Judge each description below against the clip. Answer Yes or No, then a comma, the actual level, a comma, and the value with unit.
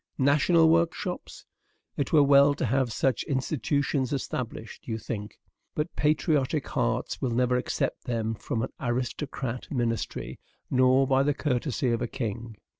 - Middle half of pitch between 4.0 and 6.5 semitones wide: No, average, 3.3 semitones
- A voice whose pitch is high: No, low, 130 Hz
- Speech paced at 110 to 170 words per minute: Yes, average, 140 wpm